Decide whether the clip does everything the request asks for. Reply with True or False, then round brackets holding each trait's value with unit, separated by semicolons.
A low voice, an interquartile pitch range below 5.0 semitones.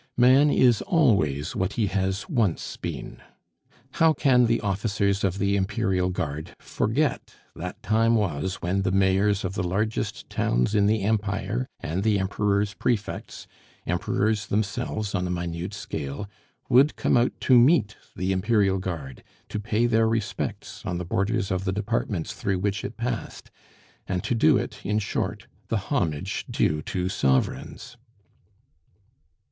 True (100 Hz; 3.3 semitones)